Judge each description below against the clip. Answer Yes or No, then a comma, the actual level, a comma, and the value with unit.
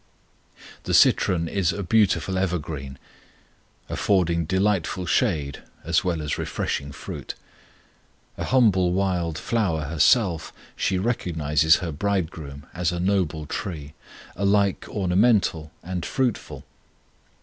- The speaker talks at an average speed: No, slow, 105 wpm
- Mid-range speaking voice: No, very low, 90 Hz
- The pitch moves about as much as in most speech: Yes, average, 3.7 semitones